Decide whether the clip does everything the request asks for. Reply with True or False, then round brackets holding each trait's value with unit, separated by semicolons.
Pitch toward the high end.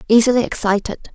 True (225 Hz)